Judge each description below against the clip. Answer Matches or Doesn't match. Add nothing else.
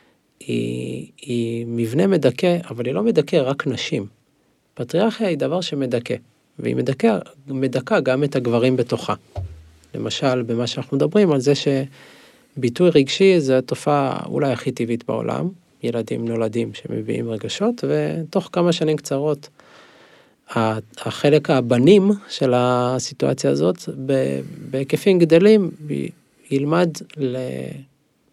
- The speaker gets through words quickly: Doesn't match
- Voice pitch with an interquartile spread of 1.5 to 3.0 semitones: Doesn't match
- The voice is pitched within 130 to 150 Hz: Matches